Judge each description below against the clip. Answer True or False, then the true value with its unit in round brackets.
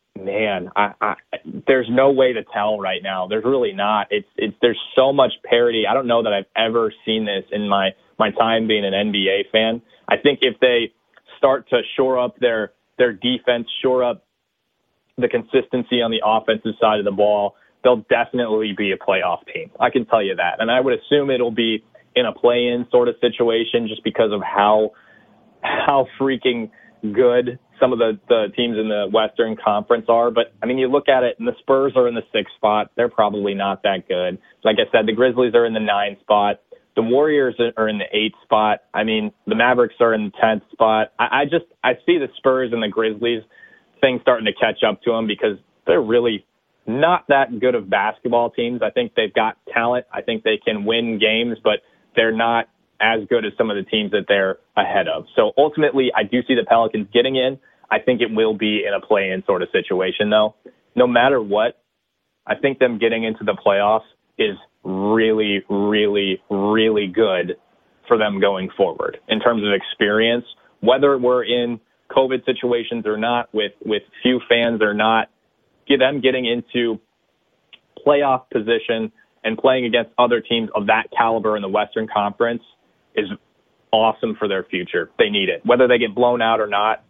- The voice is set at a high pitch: False (115 Hz)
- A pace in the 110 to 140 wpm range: False (195 wpm)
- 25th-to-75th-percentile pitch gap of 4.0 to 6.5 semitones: False (2.5 semitones)